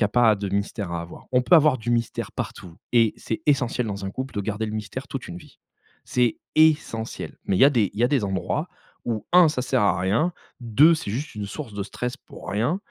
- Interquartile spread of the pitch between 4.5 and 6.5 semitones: Yes, average, 4.8 semitones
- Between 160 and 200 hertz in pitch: No, low, 115 Hz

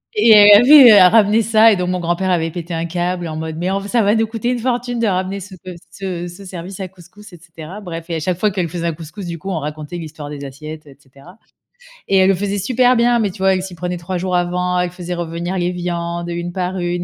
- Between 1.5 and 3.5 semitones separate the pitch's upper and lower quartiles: Yes, average, 2.8 semitones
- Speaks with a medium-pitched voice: Yes, medium, 180 Hz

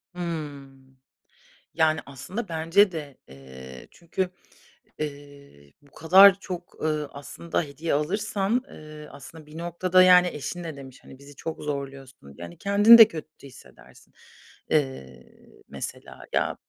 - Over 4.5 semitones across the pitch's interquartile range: No, average, 4.1 semitones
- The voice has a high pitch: No, medium, 155 Hz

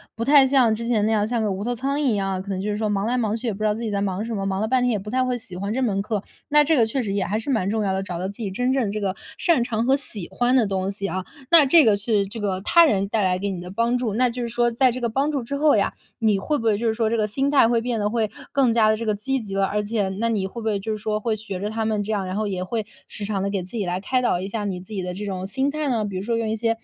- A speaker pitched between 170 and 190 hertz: No, high, 220 Hz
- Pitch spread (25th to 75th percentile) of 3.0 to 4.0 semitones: Yes, average, 3.3 semitones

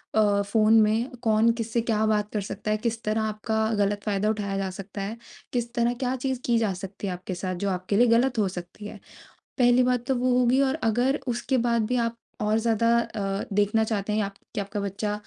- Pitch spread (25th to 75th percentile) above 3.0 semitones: No, narrow, 2.6 semitones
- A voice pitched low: No, high, 215 Hz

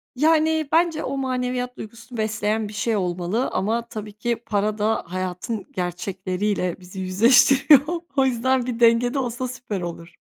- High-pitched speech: Yes, high, 225 Hz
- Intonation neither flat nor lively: Yes, average, 4.4 semitones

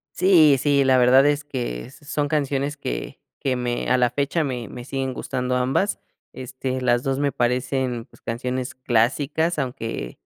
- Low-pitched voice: Yes, low, 130 Hz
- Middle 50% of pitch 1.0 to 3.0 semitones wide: Yes, narrow, 2.4 semitones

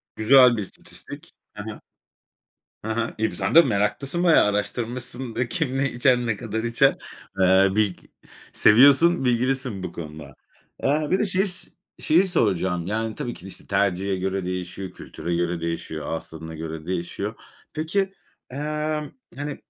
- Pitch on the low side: Yes, low, 110 Hz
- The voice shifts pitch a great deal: Yes, wide, 6.7 semitones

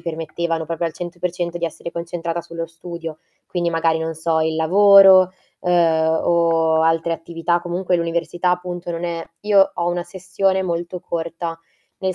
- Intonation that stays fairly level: Yes, narrow, 1.3 semitones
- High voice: No, medium, 170 Hz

